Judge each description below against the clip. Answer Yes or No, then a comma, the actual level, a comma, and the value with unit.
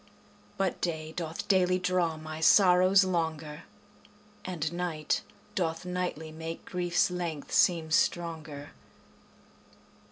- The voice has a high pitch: No, medium, 170 Hz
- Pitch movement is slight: Yes, narrow, 2.3 semitones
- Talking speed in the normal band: No, slow, 100 wpm